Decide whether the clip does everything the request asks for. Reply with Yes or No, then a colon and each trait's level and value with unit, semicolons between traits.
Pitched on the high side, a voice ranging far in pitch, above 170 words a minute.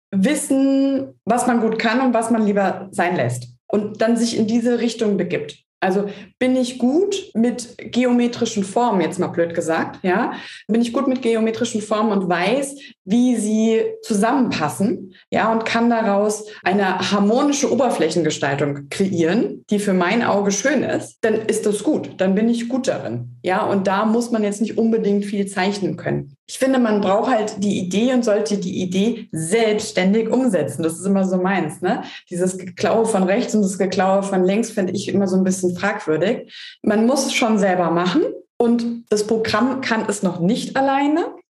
No: high, 215 Hz; average, 3.8 semitones; average, 180 wpm